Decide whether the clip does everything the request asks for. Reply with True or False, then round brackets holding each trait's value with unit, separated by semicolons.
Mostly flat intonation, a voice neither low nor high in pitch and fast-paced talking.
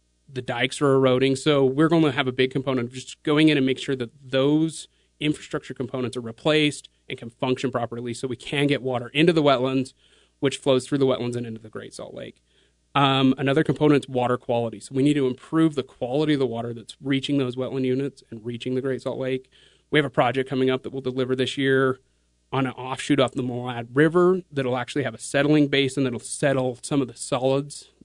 False (2.0 semitones; 130 Hz; 225 wpm)